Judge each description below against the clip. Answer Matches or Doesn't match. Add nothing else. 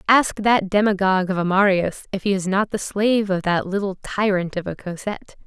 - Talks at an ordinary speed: Doesn't match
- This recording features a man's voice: Doesn't match